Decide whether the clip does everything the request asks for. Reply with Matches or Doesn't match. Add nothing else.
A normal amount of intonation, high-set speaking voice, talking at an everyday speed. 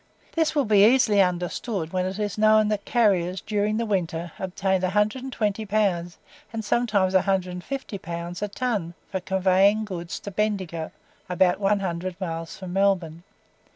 Matches